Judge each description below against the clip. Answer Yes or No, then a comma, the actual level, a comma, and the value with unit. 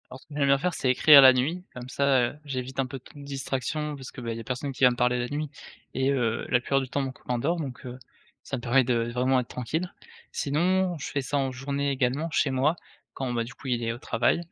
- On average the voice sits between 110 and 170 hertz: Yes, low, 135 Hz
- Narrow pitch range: Yes, narrow, 2.3 semitones